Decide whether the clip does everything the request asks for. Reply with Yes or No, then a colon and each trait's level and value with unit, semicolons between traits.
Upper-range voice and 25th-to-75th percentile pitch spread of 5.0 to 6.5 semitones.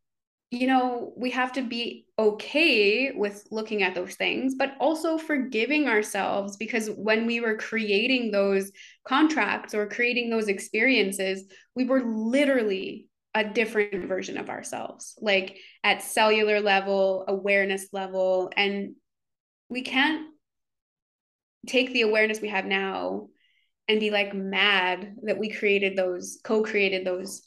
No: high, 215 Hz; average, 4.1 semitones